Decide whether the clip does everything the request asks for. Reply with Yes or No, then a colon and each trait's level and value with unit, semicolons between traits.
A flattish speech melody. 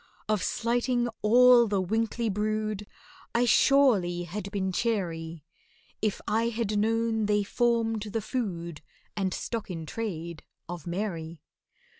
No: average, 4.3 semitones